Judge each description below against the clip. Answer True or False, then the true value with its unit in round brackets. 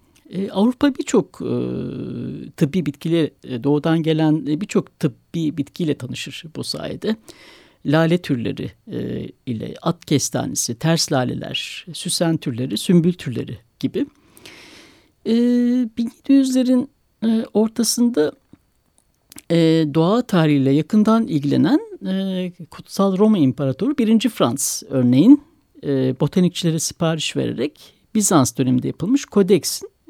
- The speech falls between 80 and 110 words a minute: True (105 wpm)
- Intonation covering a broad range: True (7.5 semitones)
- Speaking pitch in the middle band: True (165 Hz)